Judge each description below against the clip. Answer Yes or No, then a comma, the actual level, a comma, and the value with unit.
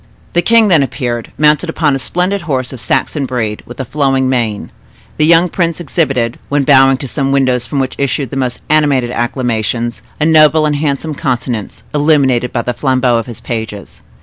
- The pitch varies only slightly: No, average, 3.7 semitones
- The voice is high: No, low, 135 Hz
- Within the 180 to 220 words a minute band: Yes, average, 185 wpm